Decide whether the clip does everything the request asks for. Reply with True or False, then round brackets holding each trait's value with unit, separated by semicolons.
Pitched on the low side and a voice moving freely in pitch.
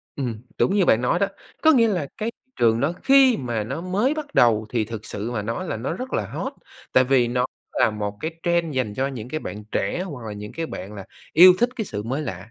True (130 Hz; 8.8 semitones)